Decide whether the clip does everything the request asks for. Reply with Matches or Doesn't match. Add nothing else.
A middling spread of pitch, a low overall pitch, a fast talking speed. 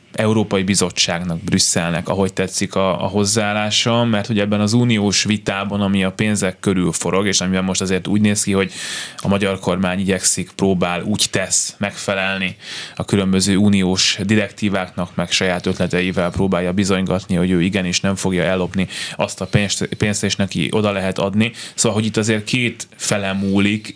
Doesn't match